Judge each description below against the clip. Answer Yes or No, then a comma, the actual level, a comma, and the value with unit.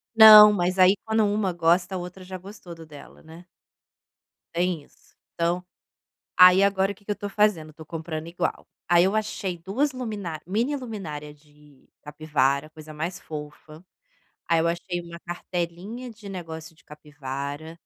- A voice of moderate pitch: Yes, medium, 175 Hz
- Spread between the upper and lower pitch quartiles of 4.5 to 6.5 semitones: No, average, 4.1 semitones